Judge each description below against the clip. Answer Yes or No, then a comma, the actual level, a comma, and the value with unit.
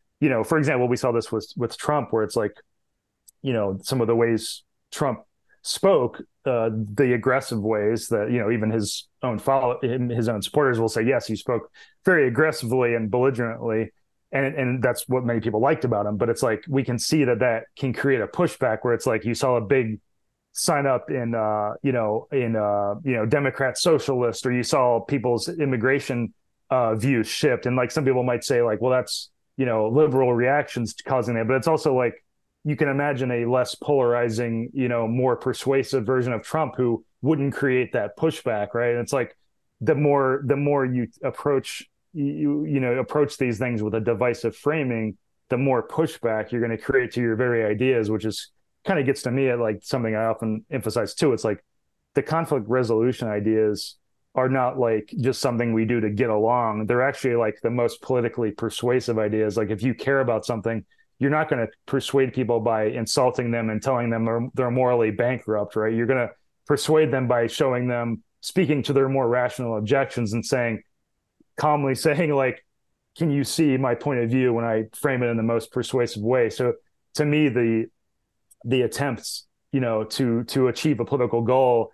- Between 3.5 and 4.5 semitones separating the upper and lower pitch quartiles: No, average, 2.9 semitones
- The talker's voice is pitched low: Yes, low, 125 Hz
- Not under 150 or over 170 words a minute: No, average, 200 wpm